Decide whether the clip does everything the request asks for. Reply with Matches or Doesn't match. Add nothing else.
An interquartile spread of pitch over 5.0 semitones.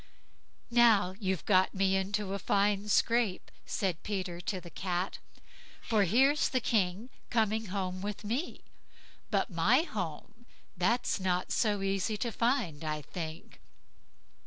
Doesn't match